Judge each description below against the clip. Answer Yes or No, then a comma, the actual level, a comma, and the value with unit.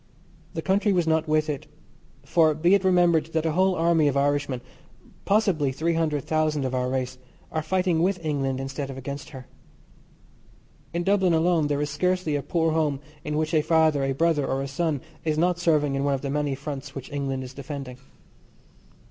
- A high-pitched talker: No, medium, 155 Hz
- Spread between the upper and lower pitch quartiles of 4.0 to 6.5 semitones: No, average, 3.2 semitones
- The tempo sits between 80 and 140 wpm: No, average, 195 wpm